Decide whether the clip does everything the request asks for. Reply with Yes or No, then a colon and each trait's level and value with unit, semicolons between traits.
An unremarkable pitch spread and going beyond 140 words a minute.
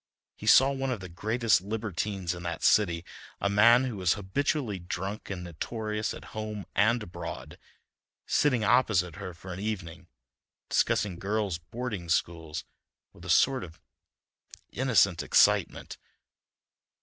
No: average, 4.2 semitones; slow, 135 wpm